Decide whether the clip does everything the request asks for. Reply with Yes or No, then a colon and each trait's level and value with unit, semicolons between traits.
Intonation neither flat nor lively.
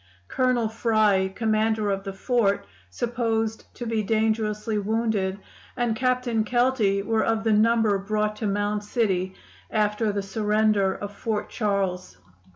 No: narrow, 1.9 semitones